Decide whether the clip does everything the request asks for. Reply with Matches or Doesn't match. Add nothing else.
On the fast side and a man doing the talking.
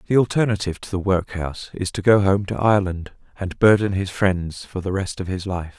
Matches